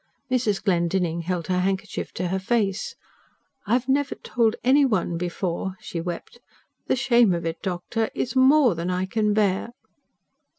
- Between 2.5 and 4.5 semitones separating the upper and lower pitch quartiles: No, average, 5.0 semitones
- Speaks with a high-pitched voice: Yes, high, 195 Hz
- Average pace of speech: Yes, average, 160 wpm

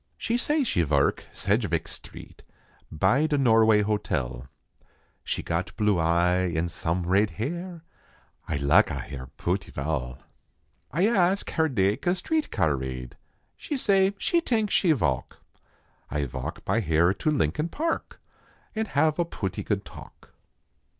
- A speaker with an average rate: Yes, average, 145 wpm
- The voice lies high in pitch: No, low, 105 Hz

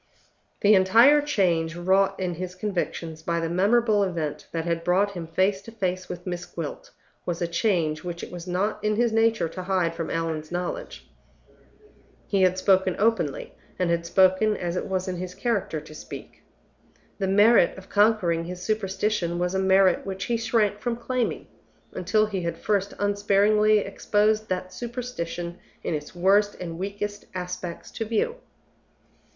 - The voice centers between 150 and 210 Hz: Yes, high, 190 Hz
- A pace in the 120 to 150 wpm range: No, average, 165 wpm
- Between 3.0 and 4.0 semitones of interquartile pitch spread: Yes, average, 3.3 semitones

